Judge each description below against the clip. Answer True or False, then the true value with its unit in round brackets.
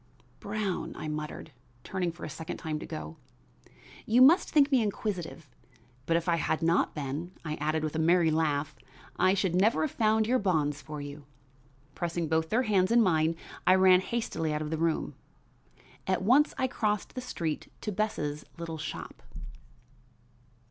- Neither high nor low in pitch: True (170 Hz)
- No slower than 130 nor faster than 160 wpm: False (170 wpm)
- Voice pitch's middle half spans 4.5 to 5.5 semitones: True (5.2 semitones)